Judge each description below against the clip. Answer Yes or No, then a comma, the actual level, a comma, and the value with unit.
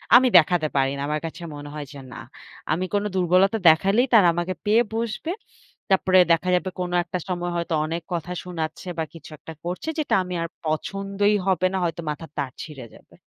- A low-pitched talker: No, medium, 175 Hz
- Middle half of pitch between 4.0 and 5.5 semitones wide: No, average, 3.2 semitones